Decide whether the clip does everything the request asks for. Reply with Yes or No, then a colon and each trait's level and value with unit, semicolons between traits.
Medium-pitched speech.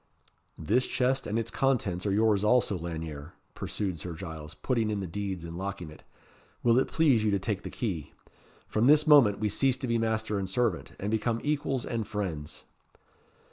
No: low, 105 Hz